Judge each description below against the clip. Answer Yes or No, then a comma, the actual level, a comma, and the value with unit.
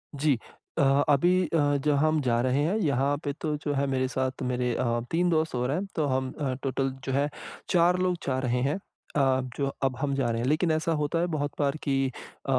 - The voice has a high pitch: No, medium, 140 Hz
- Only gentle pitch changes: No, average, 3.1 semitones